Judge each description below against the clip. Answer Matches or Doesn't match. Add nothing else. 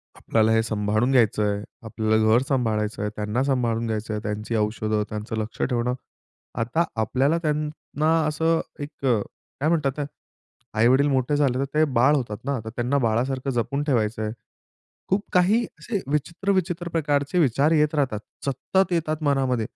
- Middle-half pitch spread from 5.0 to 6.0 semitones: Matches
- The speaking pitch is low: Matches